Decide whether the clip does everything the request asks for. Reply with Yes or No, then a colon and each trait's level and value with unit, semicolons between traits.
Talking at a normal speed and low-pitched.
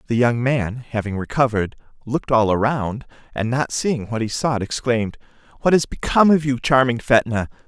Yes: average, 170 wpm; low, 120 Hz